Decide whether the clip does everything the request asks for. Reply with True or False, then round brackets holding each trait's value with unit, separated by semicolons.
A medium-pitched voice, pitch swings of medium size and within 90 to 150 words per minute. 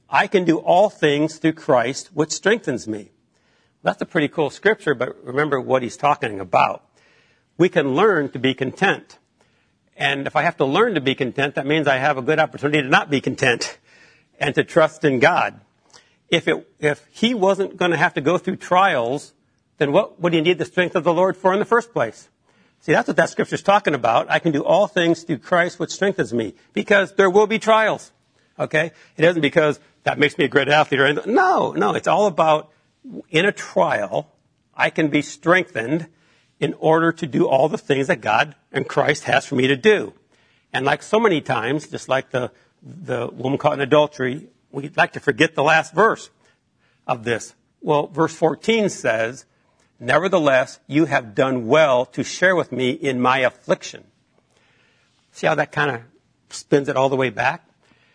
False (155 Hz; 4.1 semitones; 195 wpm)